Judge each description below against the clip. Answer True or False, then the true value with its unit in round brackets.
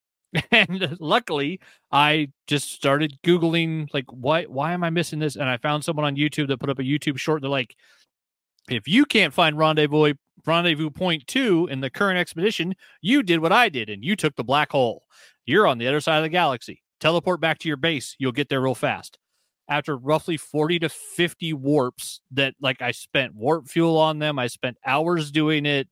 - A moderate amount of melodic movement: True (3.0 semitones)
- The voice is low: False (155 Hz)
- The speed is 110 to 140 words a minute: False (200 wpm)